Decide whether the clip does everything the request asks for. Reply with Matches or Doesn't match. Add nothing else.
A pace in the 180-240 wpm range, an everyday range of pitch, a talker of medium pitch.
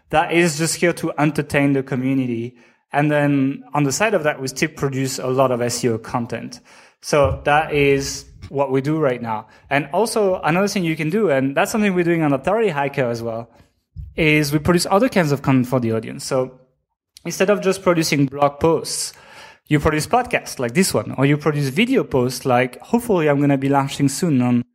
Matches